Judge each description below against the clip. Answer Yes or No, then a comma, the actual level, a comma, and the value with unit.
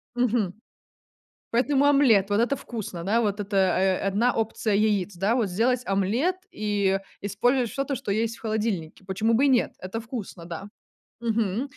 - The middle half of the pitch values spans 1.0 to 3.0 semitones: No, average, 3.6 semitones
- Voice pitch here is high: Yes, high, 215 Hz